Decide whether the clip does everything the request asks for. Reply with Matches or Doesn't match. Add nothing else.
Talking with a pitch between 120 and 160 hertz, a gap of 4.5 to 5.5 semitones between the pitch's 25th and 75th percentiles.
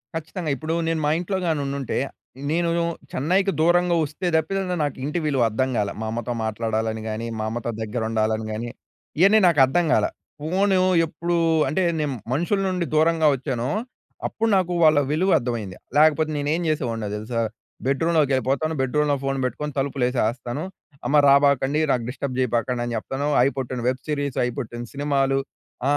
Matches